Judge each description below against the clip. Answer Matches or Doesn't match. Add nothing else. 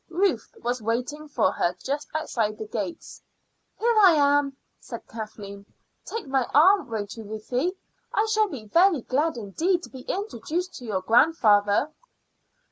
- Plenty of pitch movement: Matches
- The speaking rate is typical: Matches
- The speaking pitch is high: Matches